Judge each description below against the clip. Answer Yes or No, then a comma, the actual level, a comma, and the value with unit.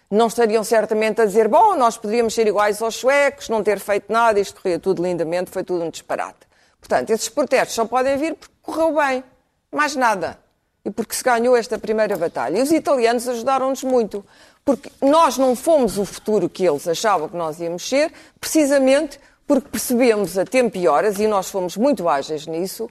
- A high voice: Yes, high, 225 Hz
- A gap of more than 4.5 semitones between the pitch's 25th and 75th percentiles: Yes, average, 4.9 semitones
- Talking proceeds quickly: Yes, fast, 190 wpm